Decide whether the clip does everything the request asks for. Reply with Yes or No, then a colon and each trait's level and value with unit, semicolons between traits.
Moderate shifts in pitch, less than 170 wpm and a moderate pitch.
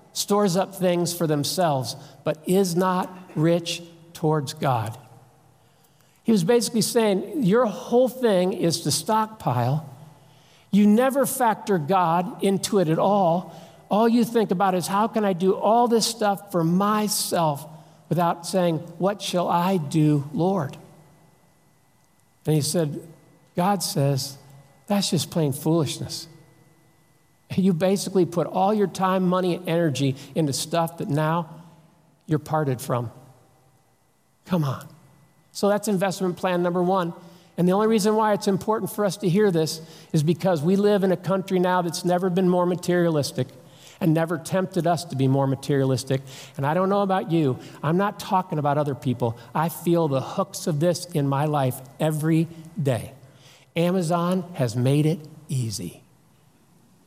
Yes: average, 3.9 semitones; average, 150 wpm; medium, 170 Hz